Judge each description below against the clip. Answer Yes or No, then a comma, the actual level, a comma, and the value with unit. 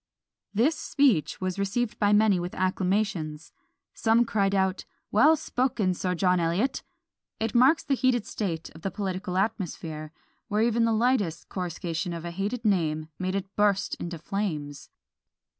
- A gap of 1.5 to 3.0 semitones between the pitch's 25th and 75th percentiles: No, average, 4.3 semitones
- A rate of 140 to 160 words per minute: Yes, average, 150 wpm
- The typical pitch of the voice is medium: No, high, 195 Hz